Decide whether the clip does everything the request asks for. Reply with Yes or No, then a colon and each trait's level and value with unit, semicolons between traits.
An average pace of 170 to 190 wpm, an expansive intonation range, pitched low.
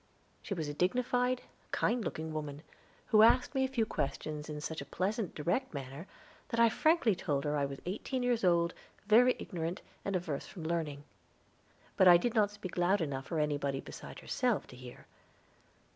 No: average, 180 wpm; wide, 7.2 semitones; medium, 175 Hz